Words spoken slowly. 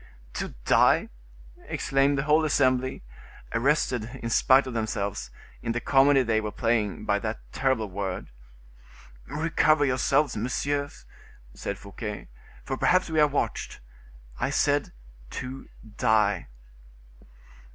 Yes: slow, 115 wpm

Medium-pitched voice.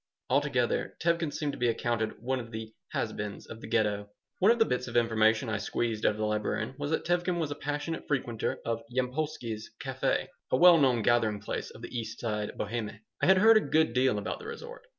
No: low, 120 Hz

